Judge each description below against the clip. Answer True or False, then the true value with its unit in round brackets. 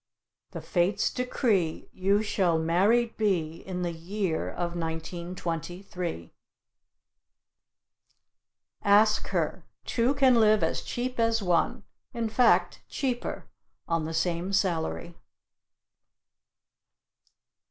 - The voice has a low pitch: False (185 Hz)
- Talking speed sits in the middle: False (95 wpm)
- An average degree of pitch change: True (4.5 semitones)